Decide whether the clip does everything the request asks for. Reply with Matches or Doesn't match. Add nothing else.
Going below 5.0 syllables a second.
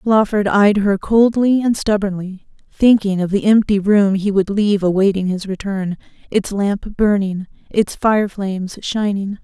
Matches